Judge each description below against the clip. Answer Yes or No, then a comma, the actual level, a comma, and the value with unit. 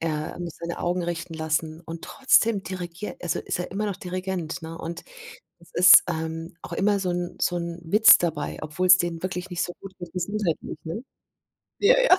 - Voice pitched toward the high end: No, medium, 175 Hz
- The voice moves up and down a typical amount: No, narrow, 2.2 semitones